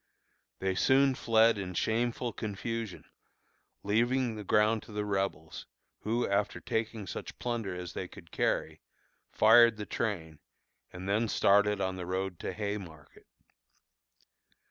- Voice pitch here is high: No, low, 105 Hz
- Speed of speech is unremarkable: No, slow, 130 wpm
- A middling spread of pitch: Yes, average, 3.1 semitones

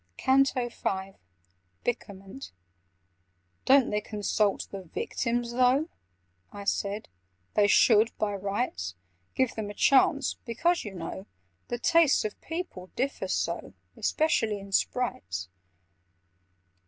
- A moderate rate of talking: No, slow, 105 wpm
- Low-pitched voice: No, high, 215 Hz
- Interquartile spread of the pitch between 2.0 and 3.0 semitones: No, average, 4.7 semitones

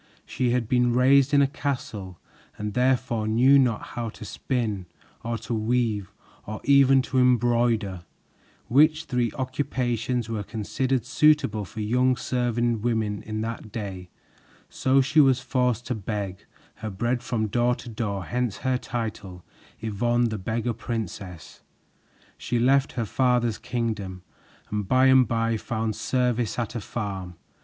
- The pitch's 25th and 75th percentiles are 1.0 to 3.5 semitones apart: Yes, average, 2.8 semitones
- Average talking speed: Yes, average, 145 wpm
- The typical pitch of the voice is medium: No, low, 120 Hz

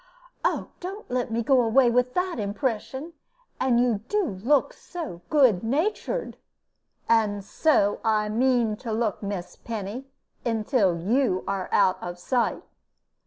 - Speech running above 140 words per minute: No, slow, 135 wpm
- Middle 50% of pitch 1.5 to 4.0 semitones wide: No, average, 4.5 semitones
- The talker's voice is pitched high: Yes, high, 235 Hz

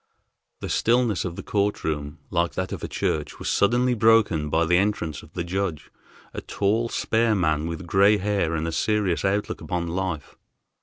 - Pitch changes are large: No, average, 4.0 semitones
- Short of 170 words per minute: No, average, 185 wpm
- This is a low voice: Yes, very low, 95 Hz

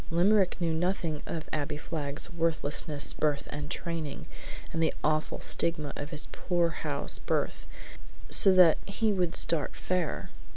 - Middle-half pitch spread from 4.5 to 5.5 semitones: No, average, 2.7 semitones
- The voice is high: No, medium, 165 Hz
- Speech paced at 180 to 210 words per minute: No, slow, 135 wpm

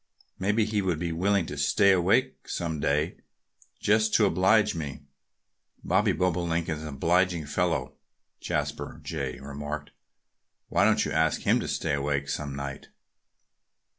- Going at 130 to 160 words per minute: Yes, average, 140 wpm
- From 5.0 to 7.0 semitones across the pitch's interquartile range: No, average, 4.6 semitones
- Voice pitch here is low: Yes, very low, 85 Hz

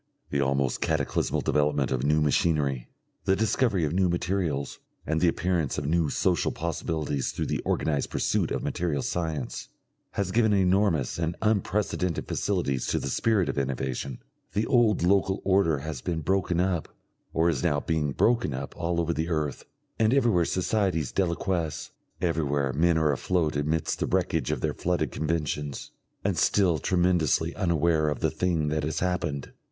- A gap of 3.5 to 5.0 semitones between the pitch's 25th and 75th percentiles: Yes, average, 3.8 semitones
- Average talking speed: Yes, average, 160 wpm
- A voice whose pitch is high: No, very low, 80 Hz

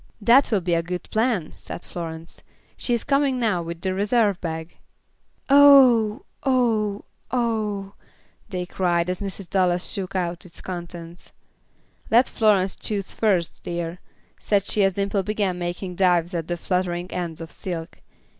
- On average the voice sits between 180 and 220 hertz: Yes, medium, 185 Hz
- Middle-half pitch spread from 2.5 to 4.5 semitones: Yes, average, 3.6 semitones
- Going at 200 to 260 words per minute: No, average, 150 wpm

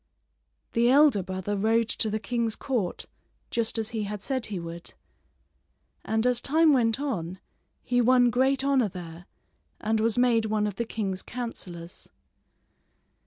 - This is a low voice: No, high, 225 Hz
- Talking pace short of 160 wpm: Yes, average, 150 wpm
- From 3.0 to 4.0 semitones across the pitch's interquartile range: Yes, average, 3.6 semitones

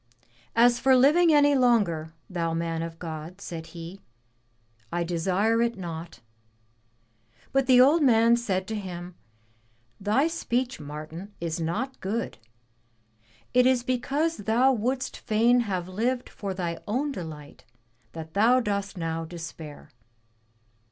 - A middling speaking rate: No, slow, 130 wpm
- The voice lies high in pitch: Yes, high, 205 Hz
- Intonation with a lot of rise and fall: Yes, wide, 6.8 semitones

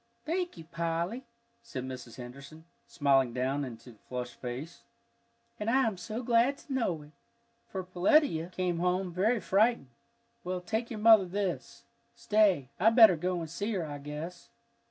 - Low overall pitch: No, medium, 180 Hz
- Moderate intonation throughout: No, wide, 7.1 semitones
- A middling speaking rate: Yes, average, 160 wpm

